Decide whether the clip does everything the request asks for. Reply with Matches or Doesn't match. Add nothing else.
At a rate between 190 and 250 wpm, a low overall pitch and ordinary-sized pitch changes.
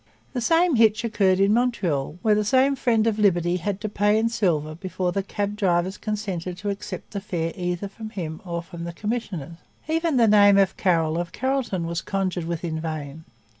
Doesn't match